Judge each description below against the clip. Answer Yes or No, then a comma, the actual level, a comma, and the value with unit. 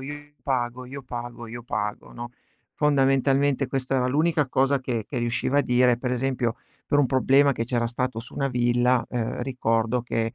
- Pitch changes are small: Yes, narrow, 2.2 semitones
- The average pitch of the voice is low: Yes, low, 125 Hz